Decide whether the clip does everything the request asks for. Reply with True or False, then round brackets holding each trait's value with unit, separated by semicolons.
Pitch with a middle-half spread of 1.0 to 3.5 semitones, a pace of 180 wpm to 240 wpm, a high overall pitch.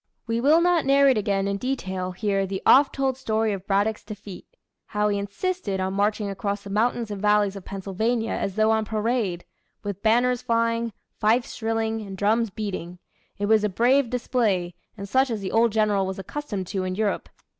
True (2.8 semitones; 190 wpm; 215 Hz)